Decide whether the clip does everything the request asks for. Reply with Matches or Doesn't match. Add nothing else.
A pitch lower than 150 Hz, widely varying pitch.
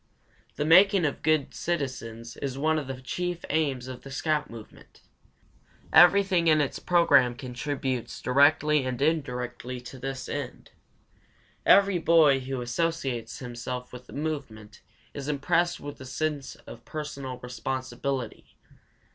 Doesn't match